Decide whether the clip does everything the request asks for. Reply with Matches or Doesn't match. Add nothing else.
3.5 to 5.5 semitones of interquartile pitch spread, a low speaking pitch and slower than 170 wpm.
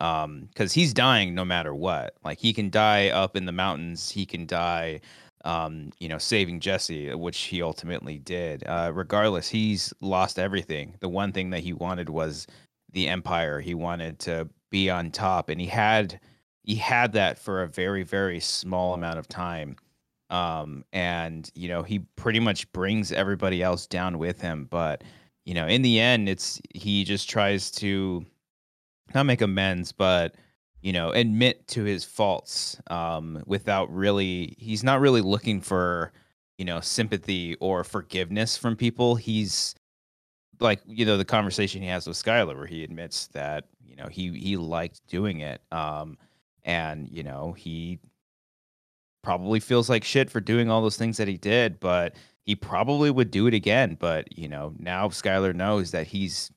Doesn't match